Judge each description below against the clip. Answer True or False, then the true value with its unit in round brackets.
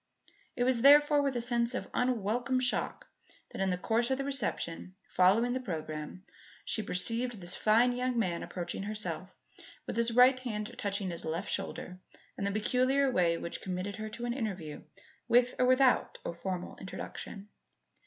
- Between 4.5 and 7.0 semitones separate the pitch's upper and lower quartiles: True (5.1 semitones)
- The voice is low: False (225 Hz)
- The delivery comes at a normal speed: True (170 wpm)